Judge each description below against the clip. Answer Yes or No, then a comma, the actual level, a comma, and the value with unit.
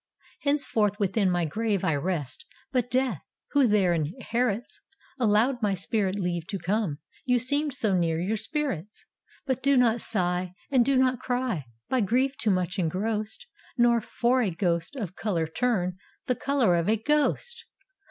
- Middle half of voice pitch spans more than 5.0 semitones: Yes, wide, 5.6 semitones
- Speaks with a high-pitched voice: Yes, high, 215 Hz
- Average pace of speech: Yes, average, 160 wpm